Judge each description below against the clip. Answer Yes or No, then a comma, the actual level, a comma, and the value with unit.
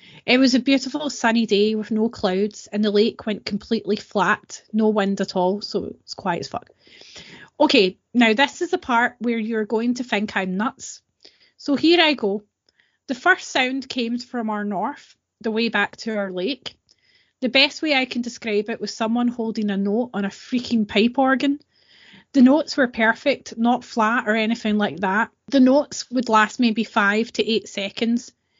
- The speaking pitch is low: No, high, 225 Hz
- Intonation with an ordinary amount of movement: Yes, average, 3.5 semitones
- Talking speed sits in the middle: Yes, average, 190 wpm